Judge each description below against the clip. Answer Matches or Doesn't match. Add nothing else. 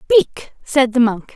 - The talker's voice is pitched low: Doesn't match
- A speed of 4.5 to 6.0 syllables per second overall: Matches